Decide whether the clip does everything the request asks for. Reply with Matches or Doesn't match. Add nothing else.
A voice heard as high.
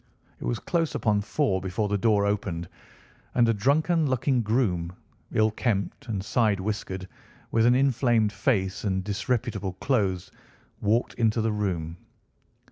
Doesn't match